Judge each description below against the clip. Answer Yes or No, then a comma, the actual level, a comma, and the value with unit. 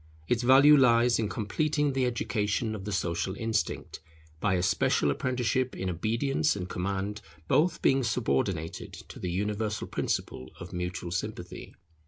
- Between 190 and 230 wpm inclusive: No, average, 145 wpm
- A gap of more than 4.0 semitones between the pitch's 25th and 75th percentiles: Yes, average, 5.3 semitones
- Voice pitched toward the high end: No, low, 110 Hz